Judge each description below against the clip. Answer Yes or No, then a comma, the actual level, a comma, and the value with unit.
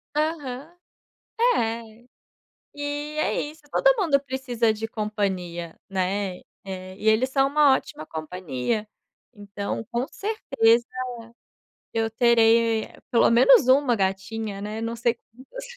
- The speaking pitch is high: Yes, high, 230 Hz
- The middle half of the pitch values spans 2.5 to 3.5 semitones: No, average, 4.7 semitones